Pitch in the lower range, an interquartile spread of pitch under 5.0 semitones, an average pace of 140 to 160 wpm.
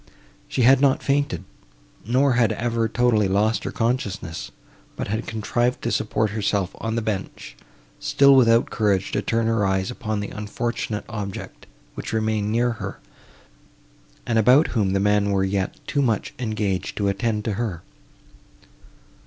Yes: low, 110 Hz; average, 2.7 semitones; average, 155 wpm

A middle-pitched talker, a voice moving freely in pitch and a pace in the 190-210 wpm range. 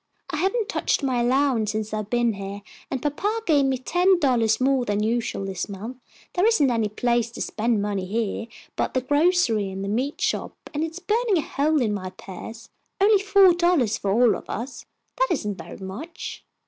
No: high, 245 Hz; wide, 7.2 semitones; average, 195 wpm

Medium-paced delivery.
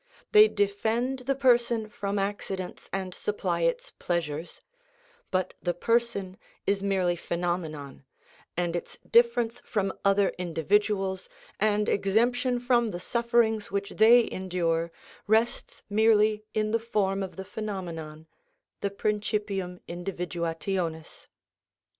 No: slow, 110 wpm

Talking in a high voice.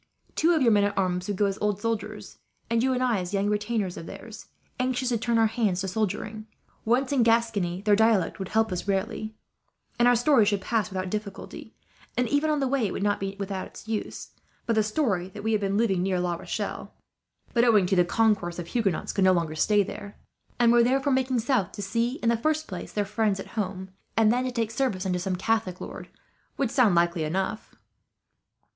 Yes: high, 210 Hz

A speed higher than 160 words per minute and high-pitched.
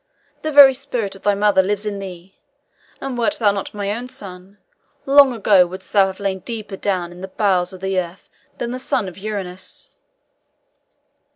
Yes: average, 180 wpm; high, 200 Hz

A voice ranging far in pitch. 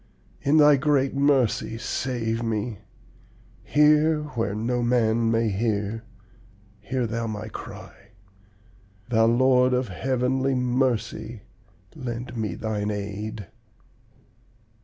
No: average, 3.0 semitones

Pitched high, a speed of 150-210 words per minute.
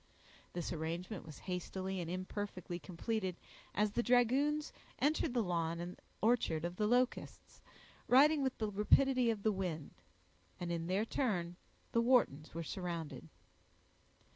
No: high, 195 Hz; average, 140 wpm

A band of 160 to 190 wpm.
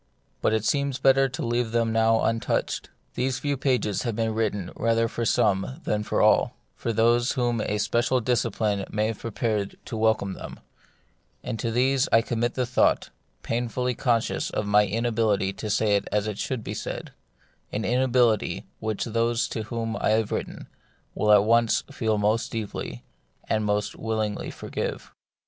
Yes: average, 170 wpm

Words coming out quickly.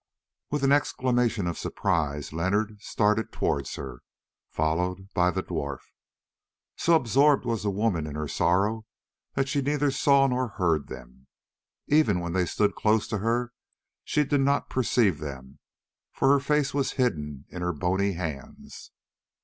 No: average, 150 wpm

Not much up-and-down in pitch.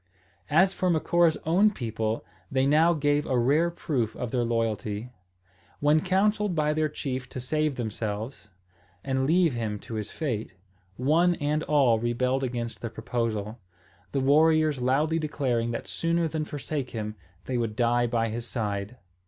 No: average, 5.1 semitones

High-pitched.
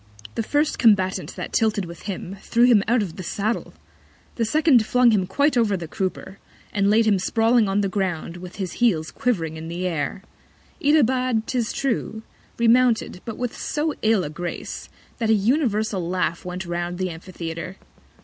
Yes: high, 205 Hz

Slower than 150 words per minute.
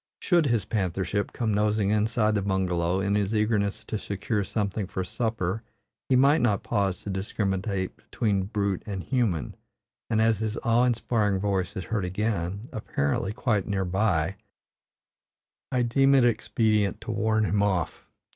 No: average, 155 wpm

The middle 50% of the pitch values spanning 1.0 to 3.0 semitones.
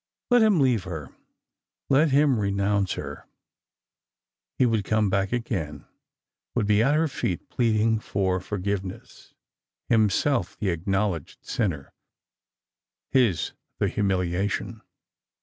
No: average, 4.0 semitones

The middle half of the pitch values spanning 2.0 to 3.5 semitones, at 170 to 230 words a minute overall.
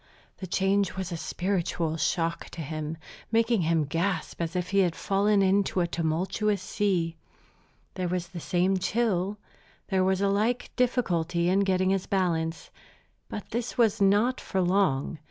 No: average, 2.9 semitones; average, 155 wpm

